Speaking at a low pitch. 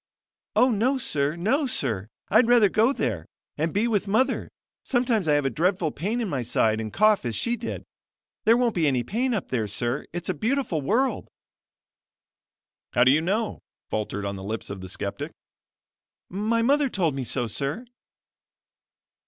No: medium, 180 Hz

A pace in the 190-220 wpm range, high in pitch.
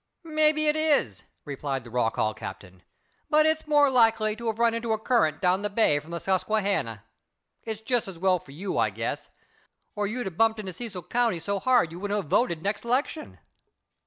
Yes: average, 200 wpm; high, 210 Hz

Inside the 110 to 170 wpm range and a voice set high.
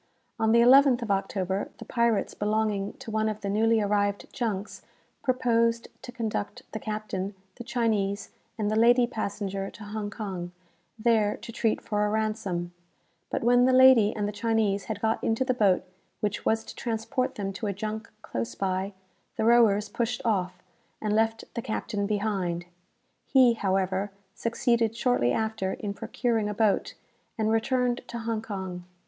Yes: average, 165 wpm; high, 215 Hz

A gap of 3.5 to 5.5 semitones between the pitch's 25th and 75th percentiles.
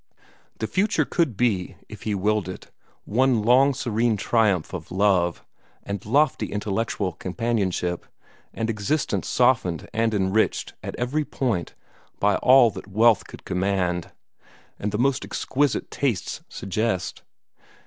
Yes: average, 4.4 semitones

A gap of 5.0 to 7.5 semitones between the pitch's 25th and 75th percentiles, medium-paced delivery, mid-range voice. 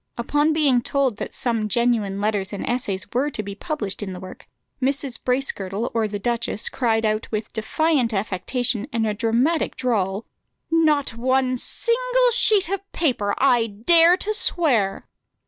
No: wide, 5.5 semitones; average, 155 wpm; high, 240 Hz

